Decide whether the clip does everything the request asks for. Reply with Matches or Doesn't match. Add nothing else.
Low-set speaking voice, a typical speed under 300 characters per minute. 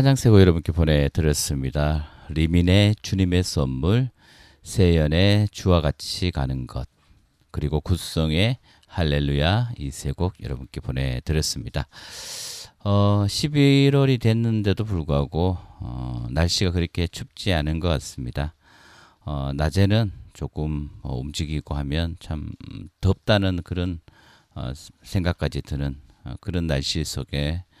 Matches